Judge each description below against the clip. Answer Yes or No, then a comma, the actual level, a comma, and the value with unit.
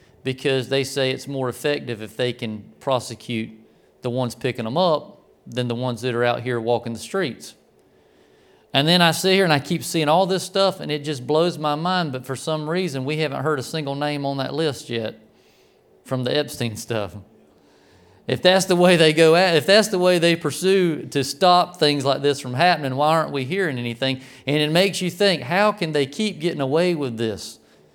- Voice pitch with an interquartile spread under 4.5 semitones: No, average, 5.3 semitones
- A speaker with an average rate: No, fast, 215 wpm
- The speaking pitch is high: No, medium, 145 Hz